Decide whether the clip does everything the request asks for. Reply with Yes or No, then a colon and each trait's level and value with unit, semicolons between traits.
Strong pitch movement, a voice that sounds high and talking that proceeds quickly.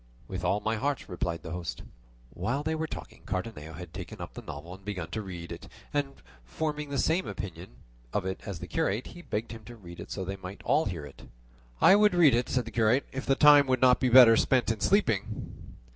No: wide, 7.2 semitones; low, 110 Hz; fast, 235 wpm